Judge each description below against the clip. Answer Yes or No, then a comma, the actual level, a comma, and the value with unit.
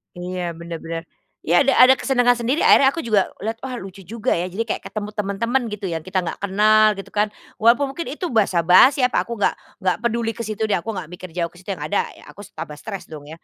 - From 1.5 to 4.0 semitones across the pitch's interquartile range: No, average, 4.6 semitones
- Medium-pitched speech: No, high, 205 Hz